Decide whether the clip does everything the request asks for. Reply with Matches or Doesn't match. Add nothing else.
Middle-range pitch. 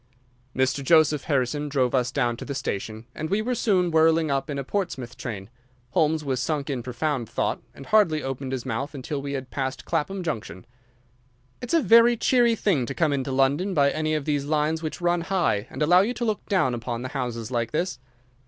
Matches